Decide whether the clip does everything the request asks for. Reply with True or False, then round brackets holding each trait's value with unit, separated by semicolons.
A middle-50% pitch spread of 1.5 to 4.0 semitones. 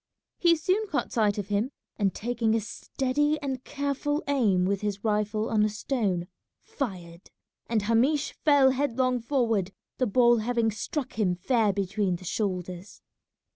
False (4.8 semitones)